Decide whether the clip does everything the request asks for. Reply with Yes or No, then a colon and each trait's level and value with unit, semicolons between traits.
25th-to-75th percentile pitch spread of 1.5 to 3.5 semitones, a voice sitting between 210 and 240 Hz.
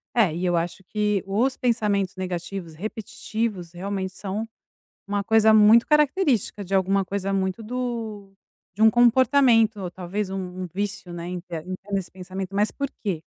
No: average, 3.1 semitones; high, 200 Hz